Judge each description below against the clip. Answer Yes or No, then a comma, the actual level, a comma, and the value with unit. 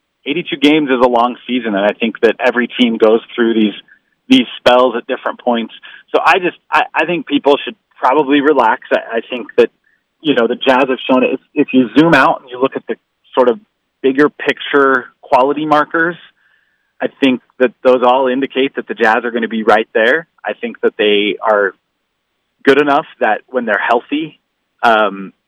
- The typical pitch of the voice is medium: No, low, 130 Hz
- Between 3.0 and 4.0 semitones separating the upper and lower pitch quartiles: Yes, average, 3.4 semitones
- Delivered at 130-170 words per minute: No, average, 200 wpm